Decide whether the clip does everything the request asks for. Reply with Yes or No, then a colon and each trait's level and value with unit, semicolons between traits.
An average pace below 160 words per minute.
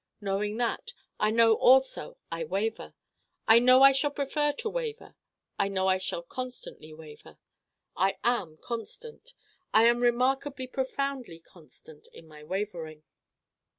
Yes: slow, 135 wpm